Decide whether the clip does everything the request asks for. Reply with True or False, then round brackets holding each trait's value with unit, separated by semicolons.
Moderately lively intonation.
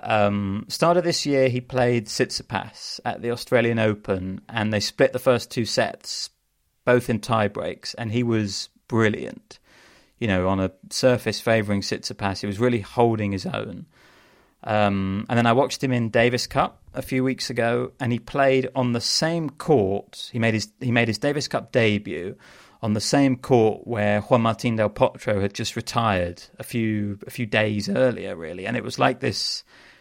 True (3.3 semitones)